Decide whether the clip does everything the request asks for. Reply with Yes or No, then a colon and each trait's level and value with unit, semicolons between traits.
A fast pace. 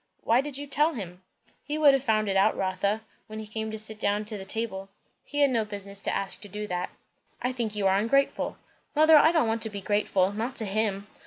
Yes: fast, 240 wpm